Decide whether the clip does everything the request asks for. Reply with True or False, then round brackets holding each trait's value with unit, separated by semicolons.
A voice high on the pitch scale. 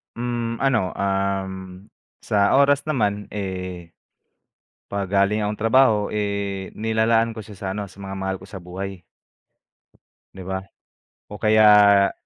False (100 Hz)